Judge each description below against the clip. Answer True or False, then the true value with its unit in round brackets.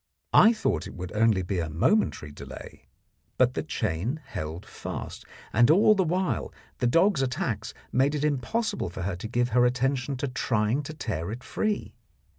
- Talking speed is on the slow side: False (175 wpm)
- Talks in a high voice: False (125 Hz)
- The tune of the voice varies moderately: False (7.3 semitones)